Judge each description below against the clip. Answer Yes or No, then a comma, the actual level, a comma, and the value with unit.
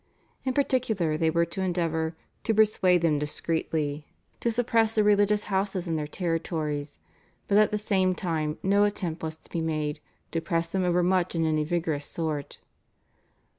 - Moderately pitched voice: Yes, medium, 170 Hz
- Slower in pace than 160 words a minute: No, average, 165 wpm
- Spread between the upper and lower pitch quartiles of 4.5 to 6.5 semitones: No, average, 4.0 semitones